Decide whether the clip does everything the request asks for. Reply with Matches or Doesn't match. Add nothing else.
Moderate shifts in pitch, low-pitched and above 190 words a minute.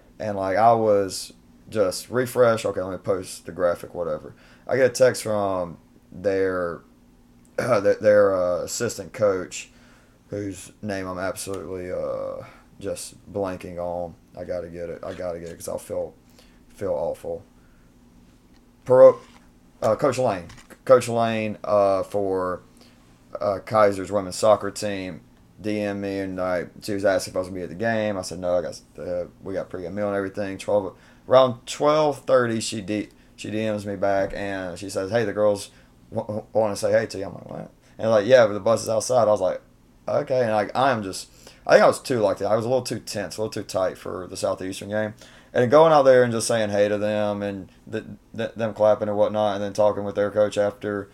Matches